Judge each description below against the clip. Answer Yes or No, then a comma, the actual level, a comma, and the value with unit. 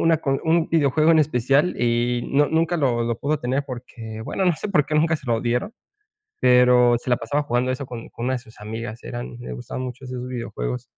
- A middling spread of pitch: Yes, average, 3.6 semitones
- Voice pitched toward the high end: No, low, 125 Hz